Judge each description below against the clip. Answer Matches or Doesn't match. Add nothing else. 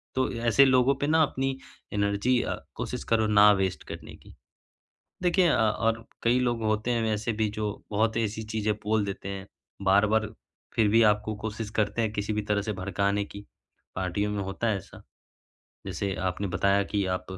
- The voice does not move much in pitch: Matches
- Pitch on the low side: Matches